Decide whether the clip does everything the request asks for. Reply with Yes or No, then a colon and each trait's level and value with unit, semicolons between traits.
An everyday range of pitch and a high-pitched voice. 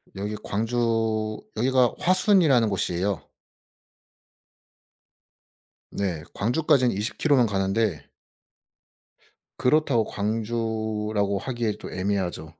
No: average, 3.4 semitones; low, 110 Hz